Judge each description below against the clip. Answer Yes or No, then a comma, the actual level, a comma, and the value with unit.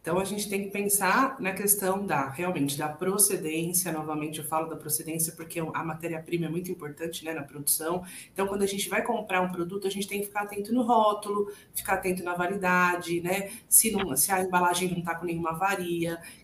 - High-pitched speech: No, medium, 180 Hz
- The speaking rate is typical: No, fast, 210 wpm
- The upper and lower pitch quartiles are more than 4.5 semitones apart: No, average, 3.2 semitones